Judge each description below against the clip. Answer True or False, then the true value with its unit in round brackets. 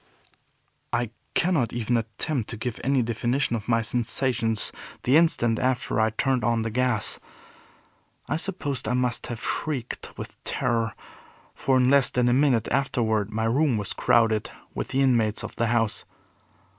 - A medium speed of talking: True (155 wpm)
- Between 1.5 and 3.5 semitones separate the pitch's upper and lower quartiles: True (2.6 semitones)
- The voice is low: True (120 Hz)